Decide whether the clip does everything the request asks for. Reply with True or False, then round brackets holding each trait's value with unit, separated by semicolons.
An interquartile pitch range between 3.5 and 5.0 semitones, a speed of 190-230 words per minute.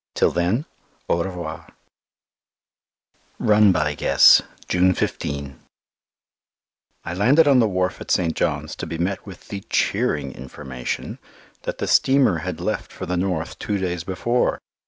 False (3.8 semitones; 140 wpm)